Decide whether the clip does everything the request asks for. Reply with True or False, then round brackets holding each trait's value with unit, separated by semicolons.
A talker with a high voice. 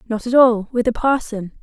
True (230 Hz)